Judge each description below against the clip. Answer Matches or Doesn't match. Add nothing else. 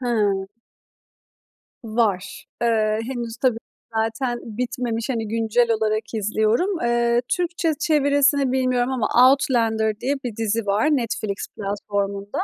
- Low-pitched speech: Doesn't match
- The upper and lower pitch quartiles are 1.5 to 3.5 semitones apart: Matches